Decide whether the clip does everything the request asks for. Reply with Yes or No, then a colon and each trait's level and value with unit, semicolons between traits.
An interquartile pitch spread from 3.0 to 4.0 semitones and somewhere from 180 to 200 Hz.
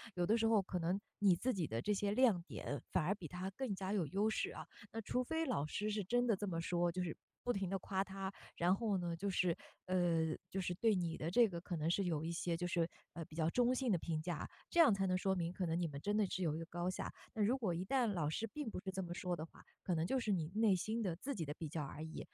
Yes: average, 3.7 semitones; medium, 185 Hz